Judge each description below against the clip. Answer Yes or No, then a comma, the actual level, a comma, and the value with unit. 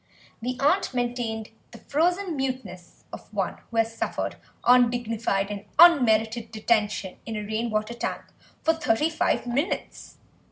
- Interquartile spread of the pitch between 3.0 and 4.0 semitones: Yes, average, 3.6 semitones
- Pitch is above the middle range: Yes, high, 235 Hz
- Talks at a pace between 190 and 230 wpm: No, slow, 135 wpm